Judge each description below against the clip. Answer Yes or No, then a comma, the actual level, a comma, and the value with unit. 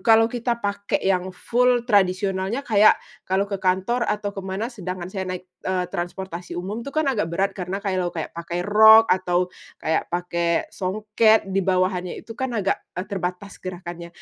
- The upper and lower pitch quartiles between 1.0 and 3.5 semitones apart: Yes, average, 3.0 semitones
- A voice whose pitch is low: No, high, 190 Hz